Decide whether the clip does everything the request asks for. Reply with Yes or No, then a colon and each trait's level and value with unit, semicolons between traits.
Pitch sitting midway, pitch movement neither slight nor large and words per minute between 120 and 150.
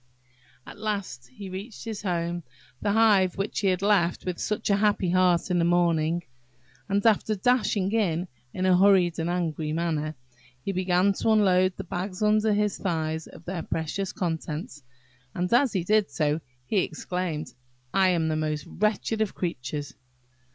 No: medium, 180 Hz; average, 3.8 semitones; average, 160 wpm